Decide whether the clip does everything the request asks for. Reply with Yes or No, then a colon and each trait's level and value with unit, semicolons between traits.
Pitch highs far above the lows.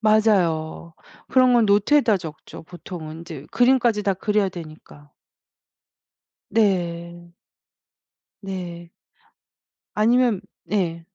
No: average, 4.3 semitones